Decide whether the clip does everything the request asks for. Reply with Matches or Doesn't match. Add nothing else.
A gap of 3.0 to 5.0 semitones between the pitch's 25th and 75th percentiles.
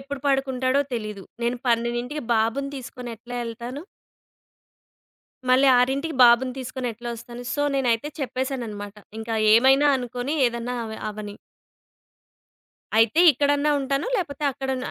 Doesn't match